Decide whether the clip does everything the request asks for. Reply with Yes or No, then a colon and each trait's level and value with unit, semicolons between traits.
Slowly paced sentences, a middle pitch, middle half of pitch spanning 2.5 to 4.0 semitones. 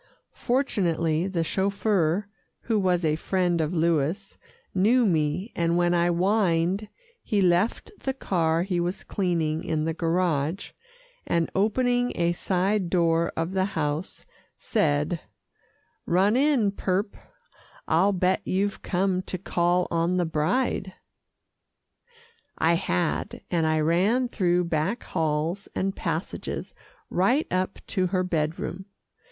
Yes: slow, 125 wpm; medium, 180 Hz; average, 3.1 semitones